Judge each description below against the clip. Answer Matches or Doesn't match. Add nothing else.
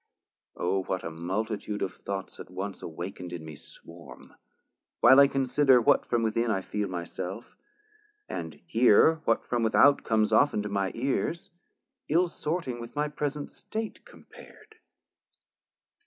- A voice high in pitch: Doesn't match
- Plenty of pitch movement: Matches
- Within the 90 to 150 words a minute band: Matches